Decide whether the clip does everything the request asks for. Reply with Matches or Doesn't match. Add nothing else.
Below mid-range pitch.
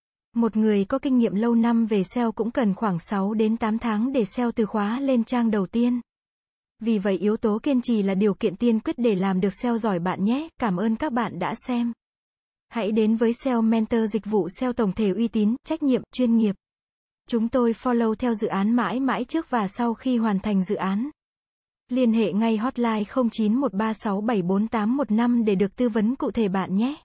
Doesn't match